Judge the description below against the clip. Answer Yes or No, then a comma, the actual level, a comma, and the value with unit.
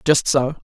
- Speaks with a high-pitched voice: No, medium, 140 Hz